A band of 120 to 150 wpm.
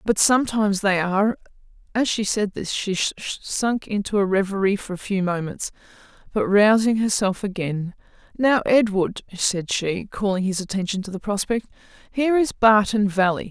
Yes: average, 145 wpm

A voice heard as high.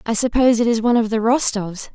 Yes: high, 225 Hz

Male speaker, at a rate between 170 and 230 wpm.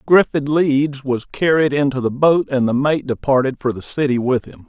Yes: male; fast, 205 wpm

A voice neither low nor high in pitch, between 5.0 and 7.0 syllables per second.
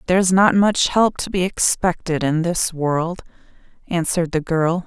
No: medium, 175 Hz; 4.4 syllables/s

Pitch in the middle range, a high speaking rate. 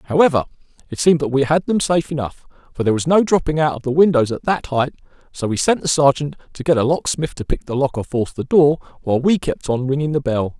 Yes: medium, 145 Hz; fast, 255 wpm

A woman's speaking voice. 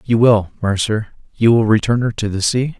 No: male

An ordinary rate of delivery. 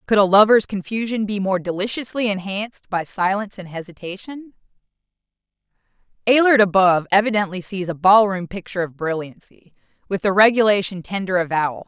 No: slow, 130 wpm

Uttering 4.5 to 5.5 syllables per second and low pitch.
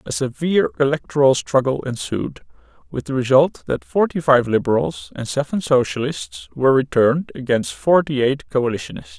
Yes: 5.4 syllables/s; low, 125 Hz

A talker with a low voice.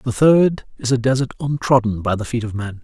Yes: low, 125 Hz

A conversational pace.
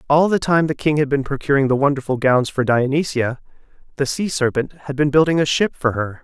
No: fast, 220 wpm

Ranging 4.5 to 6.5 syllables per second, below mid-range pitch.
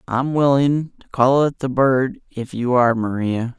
No: 4.2 syllables/s; low, 130 Hz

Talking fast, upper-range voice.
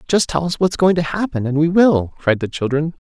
No: fast, 255 wpm; medium, 160 Hz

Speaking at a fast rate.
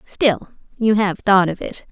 No: average, 190 wpm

